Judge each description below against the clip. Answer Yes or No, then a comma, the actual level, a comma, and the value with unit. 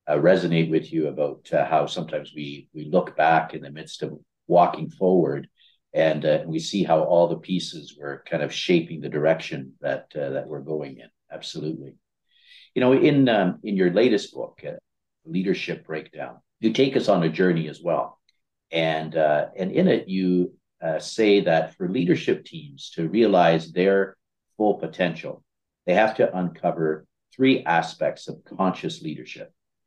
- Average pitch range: No, wide, 5.8 semitones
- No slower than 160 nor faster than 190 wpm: Yes, average, 170 wpm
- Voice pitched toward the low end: Yes, very low, 85 Hz